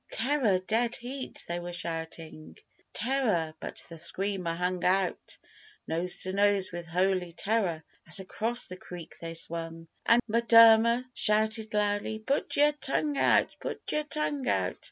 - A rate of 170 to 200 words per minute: No, average, 145 wpm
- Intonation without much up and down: No, average, 5.2 semitones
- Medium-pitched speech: No, high, 200 Hz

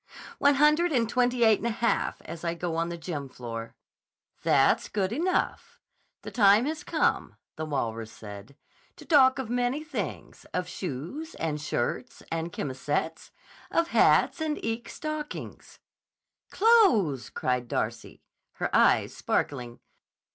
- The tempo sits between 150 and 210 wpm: No, average, 140 wpm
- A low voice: No, high, 195 Hz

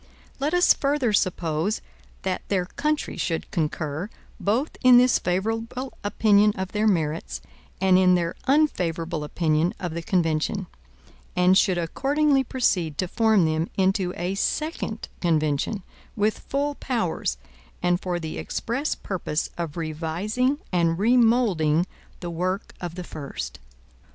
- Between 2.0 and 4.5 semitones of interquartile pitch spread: No, average, 5.3 semitones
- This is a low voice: No, medium, 185 Hz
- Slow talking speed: Yes, slow, 130 wpm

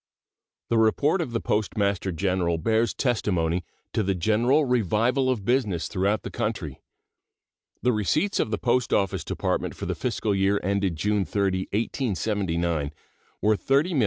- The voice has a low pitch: Yes, low, 105 Hz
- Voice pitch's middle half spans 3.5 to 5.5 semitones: Yes, average, 4.1 semitones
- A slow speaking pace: No, average, 145 wpm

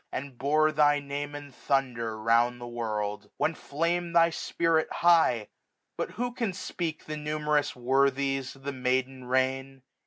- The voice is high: No, medium, 140 Hz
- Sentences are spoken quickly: No, average, 155 wpm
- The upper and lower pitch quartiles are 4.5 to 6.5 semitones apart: No, average, 3.4 semitones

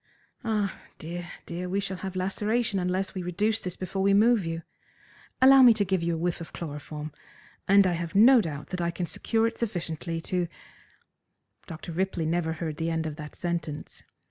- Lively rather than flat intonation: No, average, 3.2 semitones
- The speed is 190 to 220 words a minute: Yes, average, 195 wpm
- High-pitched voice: No, medium, 180 Hz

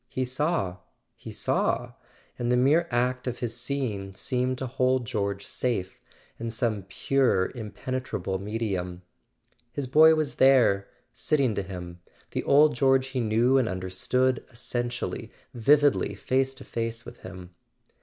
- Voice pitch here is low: Yes, low, 120 Hz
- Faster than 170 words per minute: No, average, 140 wpm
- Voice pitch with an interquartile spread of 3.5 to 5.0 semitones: Yes, average, 4.6 semitones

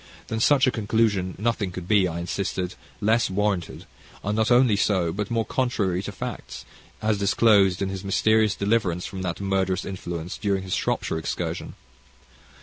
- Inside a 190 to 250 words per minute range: No, average, 160 wpm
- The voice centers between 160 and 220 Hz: No, low, 100 Hz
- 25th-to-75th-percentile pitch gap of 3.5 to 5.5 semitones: No, average, 3.0 semitones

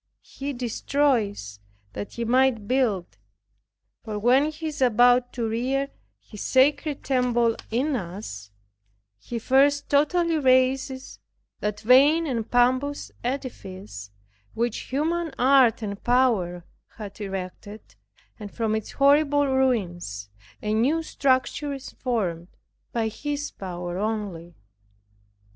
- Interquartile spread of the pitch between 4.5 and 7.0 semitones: Yes, average, 4.8 semitones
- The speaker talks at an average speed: No, slow, 115 wpm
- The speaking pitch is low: No, high, 245 Hz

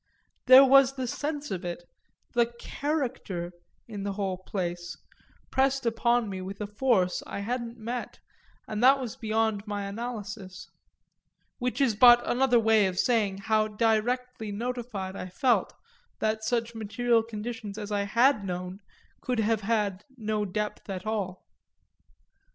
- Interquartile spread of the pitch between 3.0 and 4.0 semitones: Yes, average, 3.3 semitones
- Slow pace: No, average, 145 wpm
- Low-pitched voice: No, high, 220 Hz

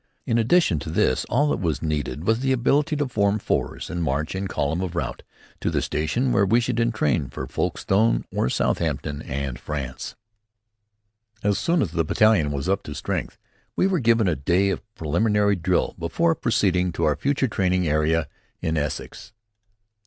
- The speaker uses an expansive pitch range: Yes, wide, 7.0 semitones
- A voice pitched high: No, very low, 95 Hz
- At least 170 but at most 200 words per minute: Yes, average, 175 wpm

